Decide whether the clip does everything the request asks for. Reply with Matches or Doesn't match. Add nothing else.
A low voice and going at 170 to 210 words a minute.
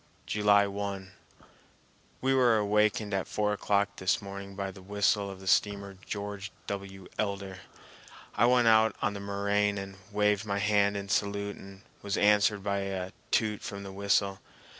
Doesn't match